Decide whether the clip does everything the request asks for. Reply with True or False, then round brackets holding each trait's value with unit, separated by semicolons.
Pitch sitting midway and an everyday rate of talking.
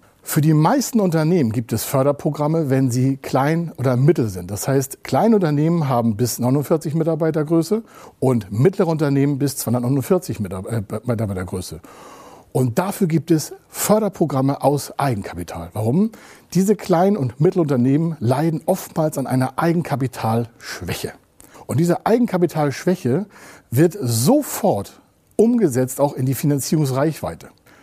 False (145 Hz; 115 wpm)